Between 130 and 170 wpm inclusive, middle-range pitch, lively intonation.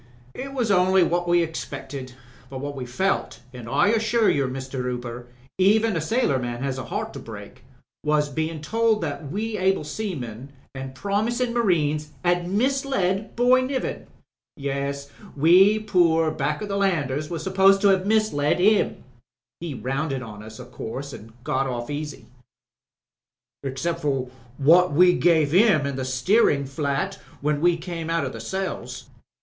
Yes: average, 155 wpm; medium, 160 Hz; wide, 6.2 semitones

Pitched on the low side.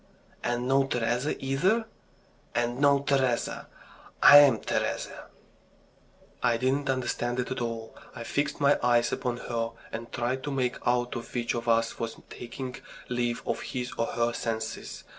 Yes: low, 125 Hz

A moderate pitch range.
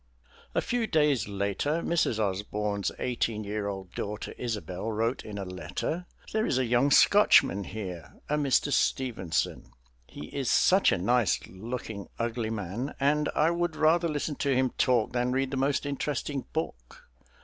No: wide, 6.0 semitones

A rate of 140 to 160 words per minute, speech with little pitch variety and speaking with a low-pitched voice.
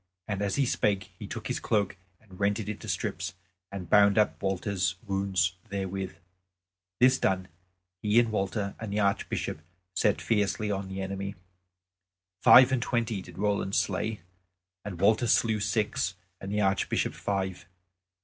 Yes: average, 150 wpm; narrow, 1.9 semitones; low, 100 Hz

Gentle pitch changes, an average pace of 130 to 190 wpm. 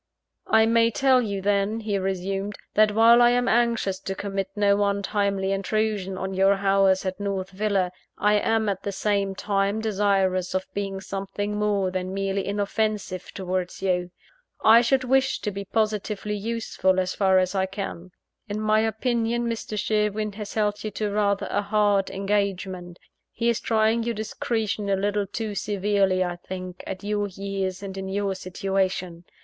Yes: narrow, 1.9 semitones; average, 165 wpm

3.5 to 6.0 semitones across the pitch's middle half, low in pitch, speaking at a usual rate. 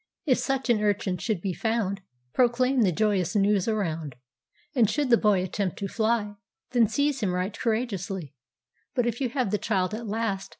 No: average, 4.2 semitones; high, 210 Hz; average, 160 wpm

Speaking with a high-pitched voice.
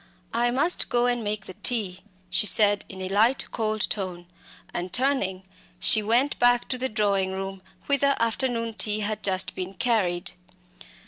Yes: high, 215 Hz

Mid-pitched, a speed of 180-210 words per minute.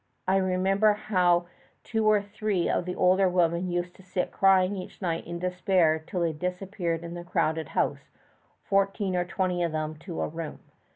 Yes: medium, 180 Hz; average, 185 wpm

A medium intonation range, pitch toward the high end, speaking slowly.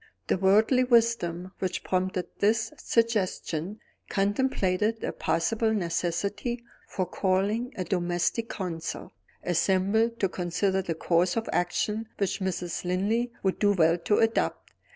Yes: average, 3.8 semitones; high, 195 Hz; slow, 125 wpm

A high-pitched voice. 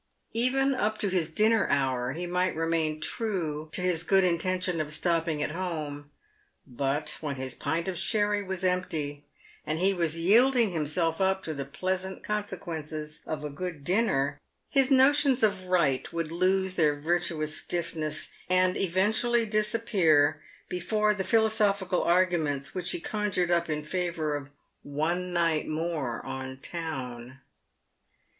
No: medium, 175 Hz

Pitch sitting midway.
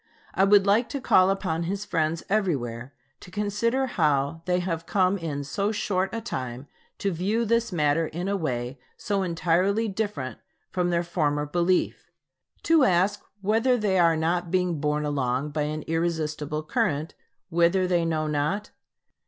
Yes: medium, 175 Hz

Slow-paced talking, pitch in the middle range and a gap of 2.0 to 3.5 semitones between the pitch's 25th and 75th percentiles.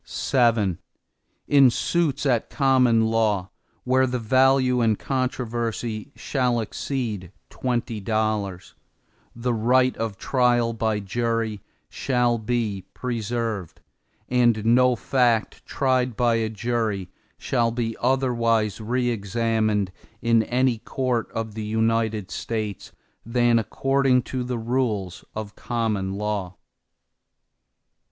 No: slow, 110 wpm; low, 115 Hz; narrow, 2.6 semitones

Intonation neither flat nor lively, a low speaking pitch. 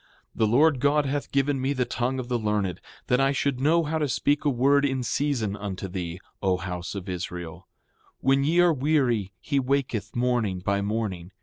No: wide, 6.0 semitones; low, 125 Hz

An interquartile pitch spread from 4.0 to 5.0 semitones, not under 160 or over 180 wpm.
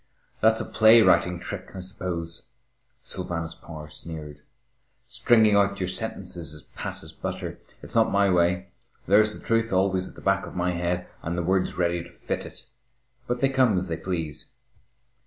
No: average, 3.1 semitones; average, 175 wpm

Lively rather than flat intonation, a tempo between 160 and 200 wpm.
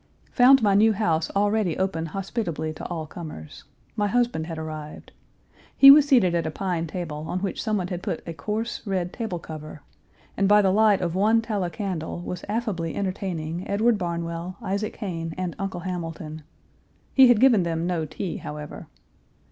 No: average, 4.1 semitones; average, 170 wpm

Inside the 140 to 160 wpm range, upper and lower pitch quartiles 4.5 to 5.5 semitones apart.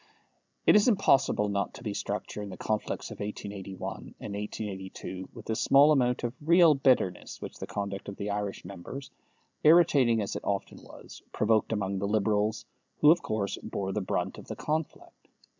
No: average, 175 wpm; average, 4.8 semitones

